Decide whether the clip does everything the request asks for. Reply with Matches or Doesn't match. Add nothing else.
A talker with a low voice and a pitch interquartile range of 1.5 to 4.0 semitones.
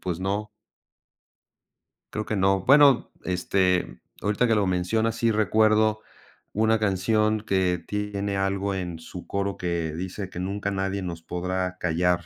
Matches